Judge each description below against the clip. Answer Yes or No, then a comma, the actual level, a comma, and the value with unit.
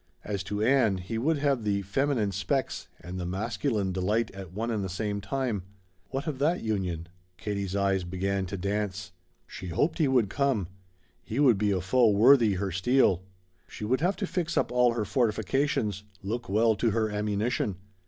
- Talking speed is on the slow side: No, average, 185 wpm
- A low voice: Yes, low, 105 Hz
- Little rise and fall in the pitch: No, average, 4.2 semitones